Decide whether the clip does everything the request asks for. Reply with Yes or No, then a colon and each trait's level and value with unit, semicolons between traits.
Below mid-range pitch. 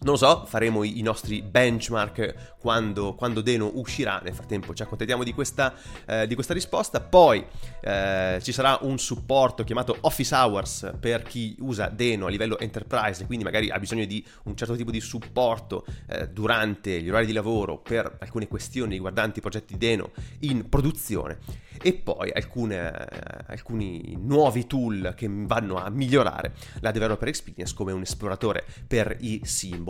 Yes: low, 110 Hz